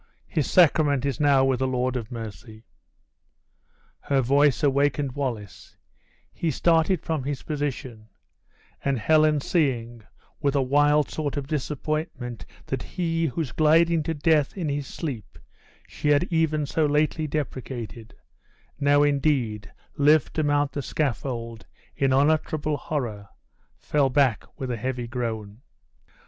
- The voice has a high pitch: No, medium, 140 Hz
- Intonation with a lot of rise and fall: No, average, 3.4 semitones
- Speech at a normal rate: No, slow, 130 wpm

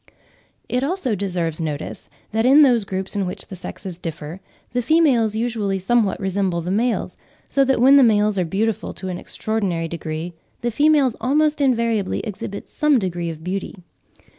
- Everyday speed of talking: Yes, average, 165 wpm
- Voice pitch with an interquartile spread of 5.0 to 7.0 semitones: Yes, wide, 5.4 semitones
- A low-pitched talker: No, high, 210 Hz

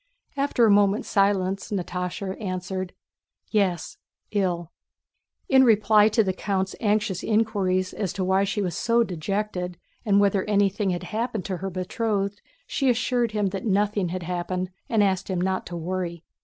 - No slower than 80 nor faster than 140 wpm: No, average, 155 wpm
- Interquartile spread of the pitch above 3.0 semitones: No, narrow, 2.4 semitones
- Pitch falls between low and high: No, high, 195 Hz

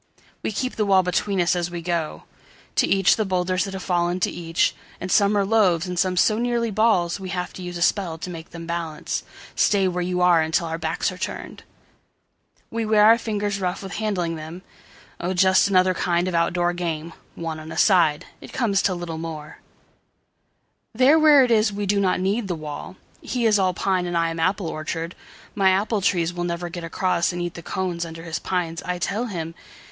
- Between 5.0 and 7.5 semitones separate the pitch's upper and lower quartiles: No, average, 2.8 semitones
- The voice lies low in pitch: No, medium, 180 Hz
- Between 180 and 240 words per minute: Yes, average, 195 wpm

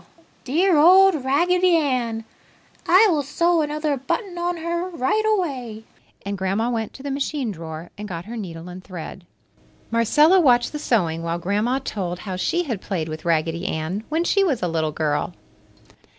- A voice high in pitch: Yes, high, 245 Hz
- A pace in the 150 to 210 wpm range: Yes, average, 170 wpm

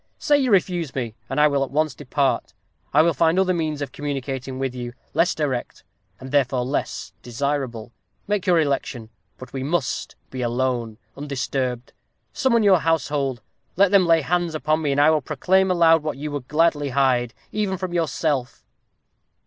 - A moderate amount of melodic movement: Yes, average, 4.1 semitones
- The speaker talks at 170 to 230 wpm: Yes, average, 175 wpm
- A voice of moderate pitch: Yes, medium, 145 Hz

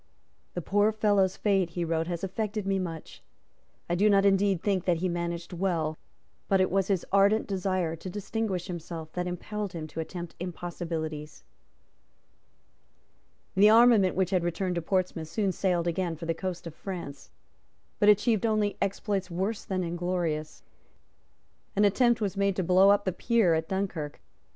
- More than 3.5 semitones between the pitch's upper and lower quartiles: No, average, 2.7 semitones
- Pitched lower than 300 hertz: Yes, medium, 185 Hz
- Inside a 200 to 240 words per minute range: No, average, 165 wpm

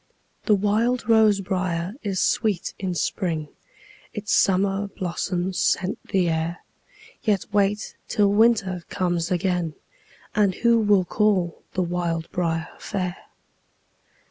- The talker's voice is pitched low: No, high, 190 Hz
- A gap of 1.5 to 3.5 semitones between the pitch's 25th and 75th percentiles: Yes, average, 2.8 semitones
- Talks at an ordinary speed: No, slow, 115 wpm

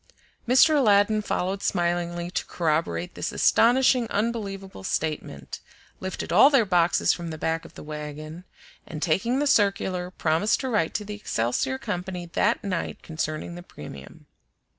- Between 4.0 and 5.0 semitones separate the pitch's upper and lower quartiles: Yes, average, 4.7 semitones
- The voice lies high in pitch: No, medium, 180 Hz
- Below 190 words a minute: Yes, average, 145 wpm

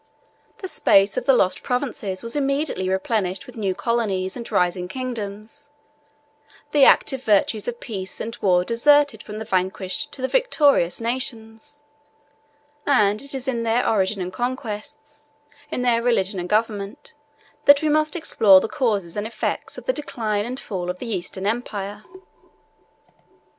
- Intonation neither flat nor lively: Yes, average, 4.8 semitones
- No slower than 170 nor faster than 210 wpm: No, average, 155 wpm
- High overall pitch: Yes, high, 225 Hz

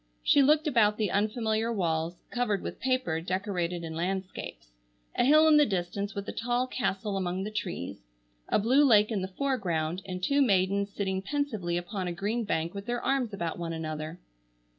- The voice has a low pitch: No, high, 200 Hz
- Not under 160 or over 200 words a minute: Yes, average, 180 wpm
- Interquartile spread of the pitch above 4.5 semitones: Yes, average, 5.1 semitones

